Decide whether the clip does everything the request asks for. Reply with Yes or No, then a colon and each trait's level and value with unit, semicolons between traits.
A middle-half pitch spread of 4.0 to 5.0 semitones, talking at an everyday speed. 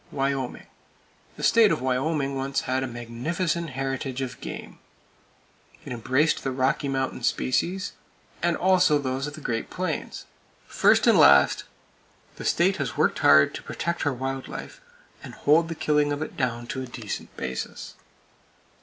No: average, 3.6 semitones; average, 155 wpm